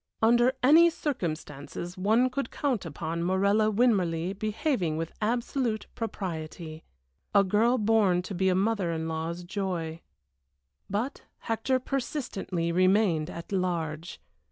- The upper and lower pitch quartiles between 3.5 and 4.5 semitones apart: No, average, 5.1 semitones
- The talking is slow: Yes, slow, 120 wpm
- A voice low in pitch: No, high, 195 Hz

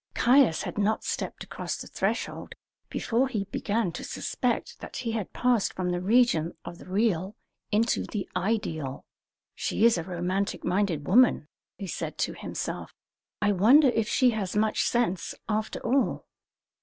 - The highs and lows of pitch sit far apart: No, average, 4.4 semitones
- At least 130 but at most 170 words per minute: Yes, average, 155 wpm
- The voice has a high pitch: Yes, high, 210 Hz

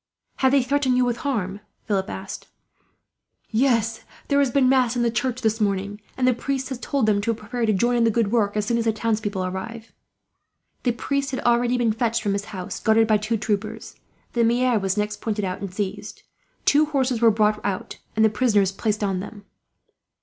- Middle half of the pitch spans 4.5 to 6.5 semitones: No, average, 3.0 semitones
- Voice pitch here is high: Yes, high, 225 Hz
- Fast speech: Yes, fast, 210 wpm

